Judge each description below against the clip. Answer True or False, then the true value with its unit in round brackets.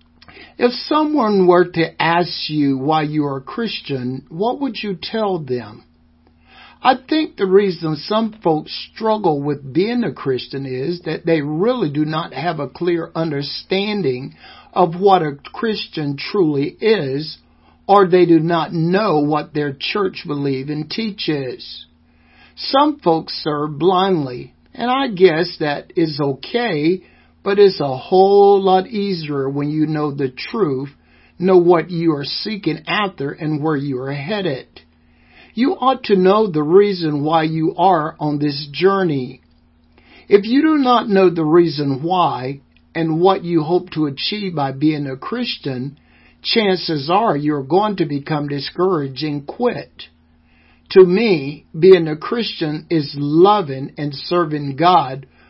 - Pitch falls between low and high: True (160 Hz)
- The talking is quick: False (145 wpm)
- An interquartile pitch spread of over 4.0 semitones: True (5.5 semitones)